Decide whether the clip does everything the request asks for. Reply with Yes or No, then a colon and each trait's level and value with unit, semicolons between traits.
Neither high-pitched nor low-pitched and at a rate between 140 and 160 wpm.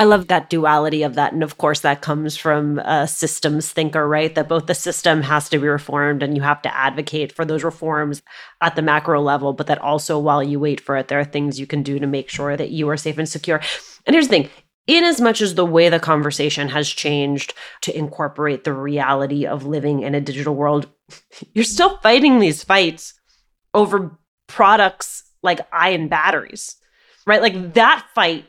No: medium, 150 Hz; fast, 205 wpm